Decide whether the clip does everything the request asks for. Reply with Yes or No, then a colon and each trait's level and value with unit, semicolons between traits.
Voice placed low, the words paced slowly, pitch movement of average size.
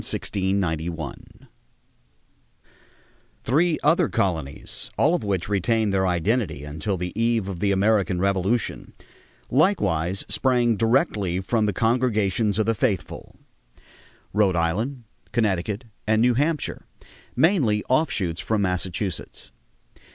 Yes: low, 105 Hz; slow, 115 wpm; average, 4.3 semitones